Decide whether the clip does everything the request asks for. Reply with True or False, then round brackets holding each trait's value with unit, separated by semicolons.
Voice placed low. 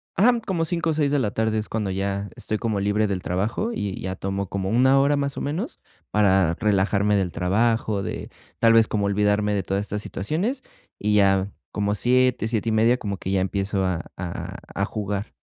True (105 Hz)